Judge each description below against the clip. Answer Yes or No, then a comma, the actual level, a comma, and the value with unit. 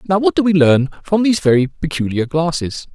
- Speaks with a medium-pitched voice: Yes, medium, 165 Hz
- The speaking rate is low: No, fast, 205 wpm